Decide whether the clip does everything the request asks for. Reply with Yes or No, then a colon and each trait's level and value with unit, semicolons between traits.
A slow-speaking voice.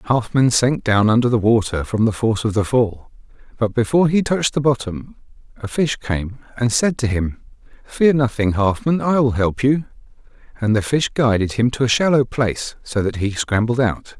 No: average, 195 wpm